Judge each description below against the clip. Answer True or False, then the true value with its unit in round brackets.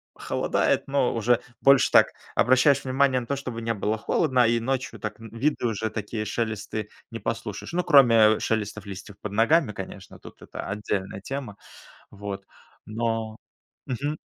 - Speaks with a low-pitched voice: True (115 Hz)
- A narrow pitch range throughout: False (3.8 semitones)